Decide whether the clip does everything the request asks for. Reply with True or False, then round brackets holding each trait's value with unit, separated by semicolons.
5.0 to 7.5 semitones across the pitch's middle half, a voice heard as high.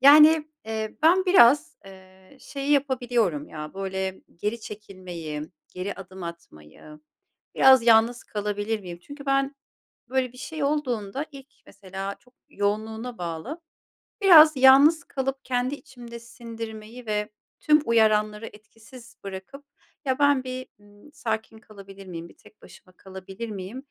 True (5.4 semitones; 225 Hz)